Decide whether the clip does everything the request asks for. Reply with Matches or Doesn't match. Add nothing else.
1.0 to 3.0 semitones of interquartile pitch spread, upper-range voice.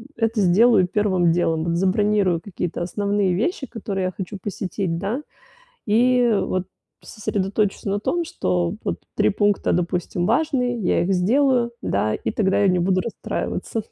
Doesn't match